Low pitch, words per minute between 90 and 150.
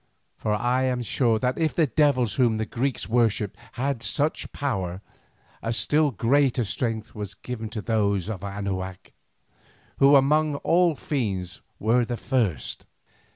Yes: low, 115 Hz; average, 145 wpm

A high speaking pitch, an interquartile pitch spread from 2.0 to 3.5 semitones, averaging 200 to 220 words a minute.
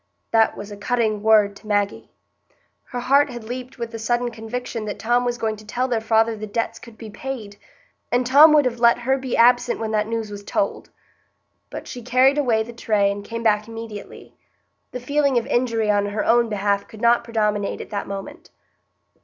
Yes: high, 230 Hz; narrow, 2.6 semitones; fast, 205 wpm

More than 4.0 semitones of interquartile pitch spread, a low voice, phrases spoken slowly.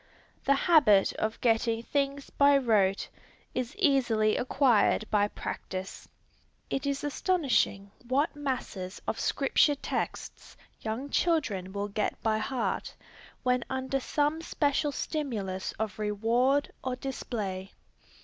No: average, 5.0 semitones; very high, 250 Hz; slow, 115 wpm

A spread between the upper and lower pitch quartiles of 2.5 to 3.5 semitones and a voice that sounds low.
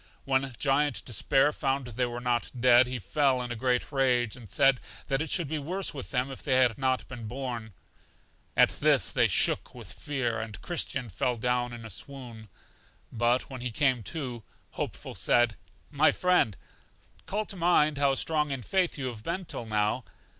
Yes: average, 2.8 semitones; low, 130 Hz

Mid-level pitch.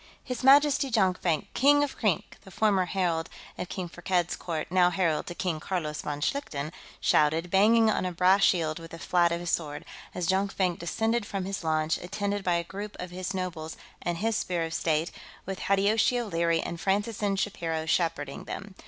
Yes: medium, 180 Hz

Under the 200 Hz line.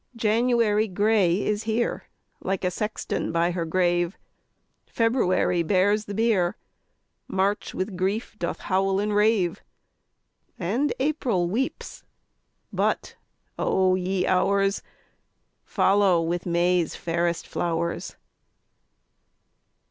Yes: high, 190 Hz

